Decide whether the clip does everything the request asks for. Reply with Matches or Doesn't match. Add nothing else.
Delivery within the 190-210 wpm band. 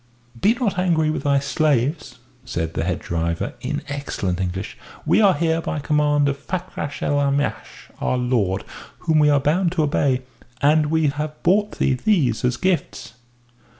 Doesn't match